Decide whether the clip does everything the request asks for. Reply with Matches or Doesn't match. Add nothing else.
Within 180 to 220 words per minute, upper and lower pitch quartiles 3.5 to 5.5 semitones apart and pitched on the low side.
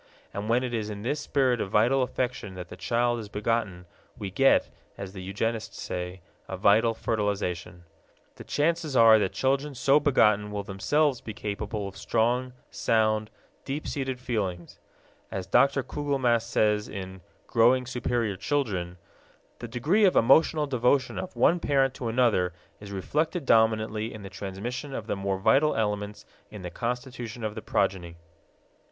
Doesn't match